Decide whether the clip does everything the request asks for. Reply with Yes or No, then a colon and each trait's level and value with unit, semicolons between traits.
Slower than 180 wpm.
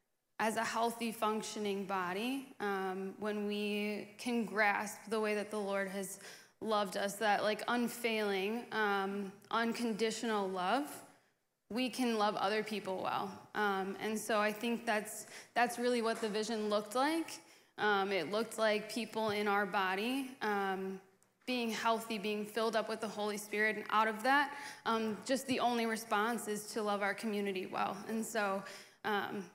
Yes: average, 160 wpm